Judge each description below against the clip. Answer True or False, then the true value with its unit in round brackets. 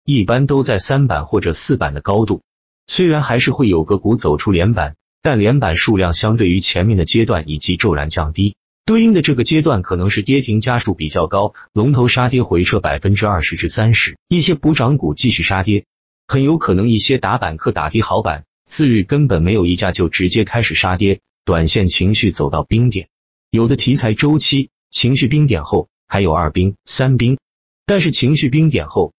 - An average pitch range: False (6.7 semitones)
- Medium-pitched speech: False (110 Hz)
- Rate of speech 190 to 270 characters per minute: False (295 characters per minute)